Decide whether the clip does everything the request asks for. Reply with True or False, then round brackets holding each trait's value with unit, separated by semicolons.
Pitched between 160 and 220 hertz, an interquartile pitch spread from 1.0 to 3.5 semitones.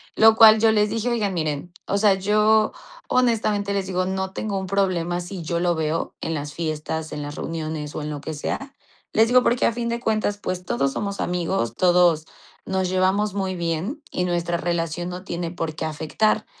False (185 Hz; 4.1 semitones)